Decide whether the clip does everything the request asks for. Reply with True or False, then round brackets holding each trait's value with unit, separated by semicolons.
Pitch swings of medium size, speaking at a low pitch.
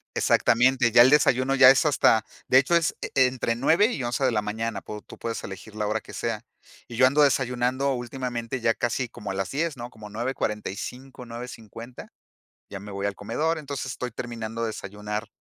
True (3.3 semitones; 120 Hz)